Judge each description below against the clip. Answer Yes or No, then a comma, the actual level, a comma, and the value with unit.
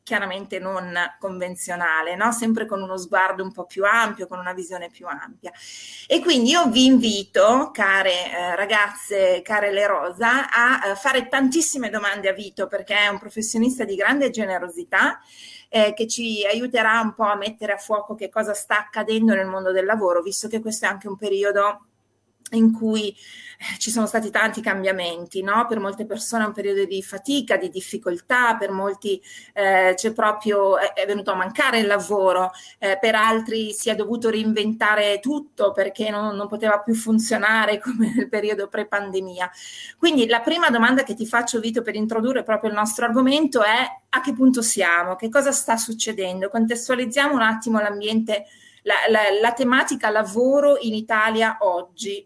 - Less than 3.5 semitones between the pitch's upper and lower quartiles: Yes, average, 2.8 semitones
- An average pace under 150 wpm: No, fast, 170 wpm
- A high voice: Yes, high, 215 Hz